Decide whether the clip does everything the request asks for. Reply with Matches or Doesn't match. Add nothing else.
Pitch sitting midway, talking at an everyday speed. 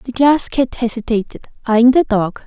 Doesn't match